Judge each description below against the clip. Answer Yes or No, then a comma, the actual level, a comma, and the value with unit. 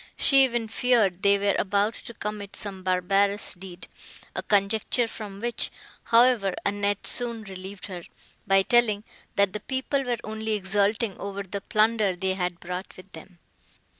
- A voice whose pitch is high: Yes, high, 200 Hz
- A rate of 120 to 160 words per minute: Yes, average, 155 wpm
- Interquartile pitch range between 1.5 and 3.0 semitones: Yes, narrow, 2.6 semitones